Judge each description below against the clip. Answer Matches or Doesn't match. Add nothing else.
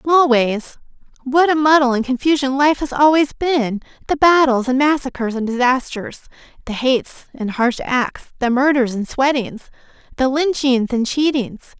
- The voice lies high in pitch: Matches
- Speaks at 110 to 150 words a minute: Matches